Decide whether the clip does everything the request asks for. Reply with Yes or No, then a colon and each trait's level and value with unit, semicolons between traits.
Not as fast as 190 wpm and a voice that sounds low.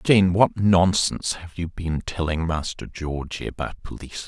Yes: average, 155 wpm; very low, 85 Hz